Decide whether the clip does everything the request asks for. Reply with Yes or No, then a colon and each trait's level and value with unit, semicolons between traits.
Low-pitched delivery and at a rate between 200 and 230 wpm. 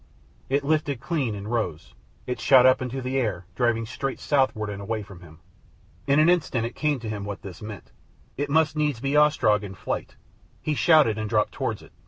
Yes: low, 125 Hz; fast, 205 wpm